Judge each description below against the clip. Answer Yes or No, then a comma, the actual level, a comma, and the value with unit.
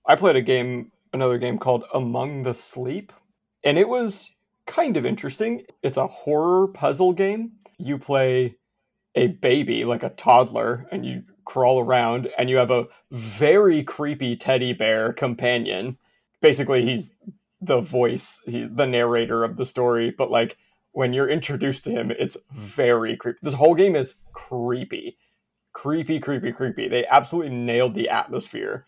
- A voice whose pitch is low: Yes, low, 130 Hz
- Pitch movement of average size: Yes, average, 4.0 semitones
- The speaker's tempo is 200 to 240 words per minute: No, average, 155 wpm